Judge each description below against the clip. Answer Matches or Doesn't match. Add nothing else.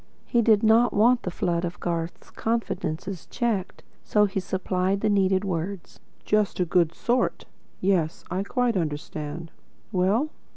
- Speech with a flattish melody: Doesn't match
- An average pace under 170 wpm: Matches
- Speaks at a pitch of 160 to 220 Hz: Matches